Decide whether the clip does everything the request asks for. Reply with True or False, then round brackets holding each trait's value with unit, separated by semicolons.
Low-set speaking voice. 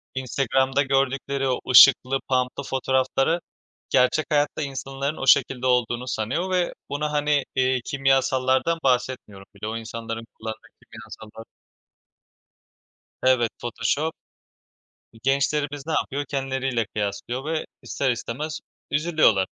True (130 Hz)